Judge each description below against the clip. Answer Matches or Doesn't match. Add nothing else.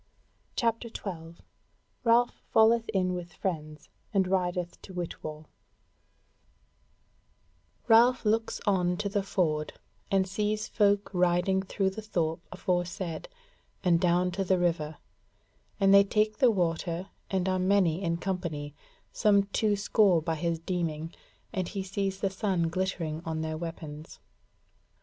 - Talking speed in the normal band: Doesn't match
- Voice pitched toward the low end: Doesn't match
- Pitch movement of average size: Matches